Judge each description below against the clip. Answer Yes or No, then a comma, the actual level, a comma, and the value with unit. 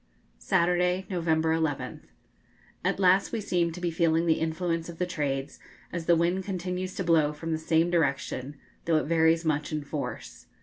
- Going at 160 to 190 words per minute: Yes, average, 175 wpm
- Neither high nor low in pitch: Yes, medium, 165 Hz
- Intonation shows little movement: Yes, narrow, 2.0 semitones